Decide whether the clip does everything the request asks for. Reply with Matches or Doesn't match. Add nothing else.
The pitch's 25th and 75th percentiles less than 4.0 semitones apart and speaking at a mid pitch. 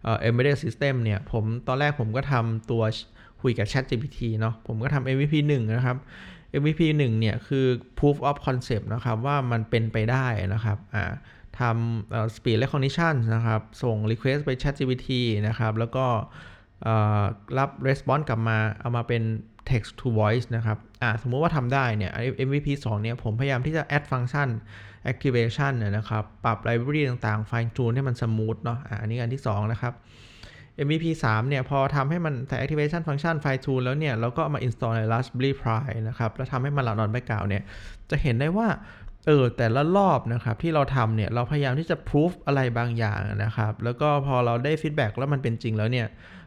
Doesn't match